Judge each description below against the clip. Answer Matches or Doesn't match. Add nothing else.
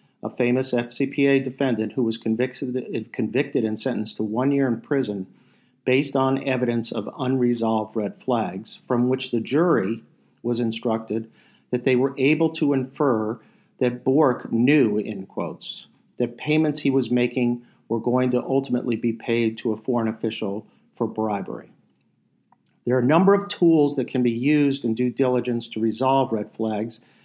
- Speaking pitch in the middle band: Doesn't match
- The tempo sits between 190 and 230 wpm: Doesn't match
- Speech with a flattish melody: Doesn't match